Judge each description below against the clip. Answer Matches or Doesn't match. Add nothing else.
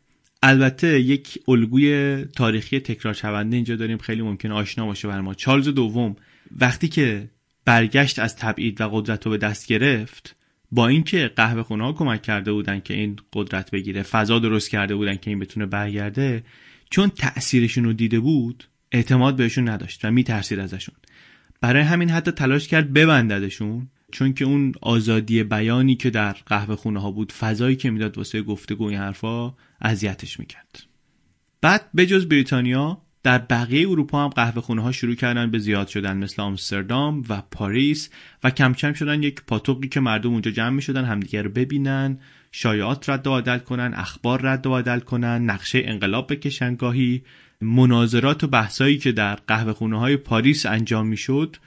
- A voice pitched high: Doesn't match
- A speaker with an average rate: Doesn't match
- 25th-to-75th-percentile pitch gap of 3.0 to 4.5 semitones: Matches